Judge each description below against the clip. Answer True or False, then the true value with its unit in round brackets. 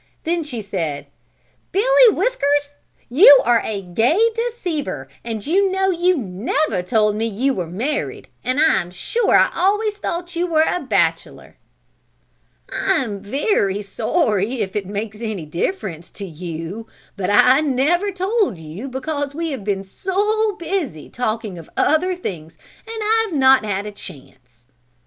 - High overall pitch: True (260 Hz)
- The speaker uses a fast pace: False (155 wpm)